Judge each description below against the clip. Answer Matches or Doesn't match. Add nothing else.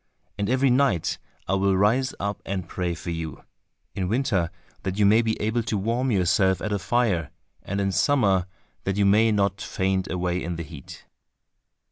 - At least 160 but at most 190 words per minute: Matches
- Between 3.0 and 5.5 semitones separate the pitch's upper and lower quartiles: Matches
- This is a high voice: Doesn't match